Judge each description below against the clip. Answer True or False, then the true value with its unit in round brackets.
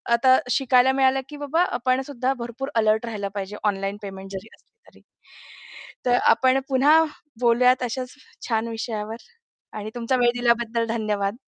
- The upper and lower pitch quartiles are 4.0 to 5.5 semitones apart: False (3.2 semitones)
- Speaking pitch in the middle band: False (235 Hz)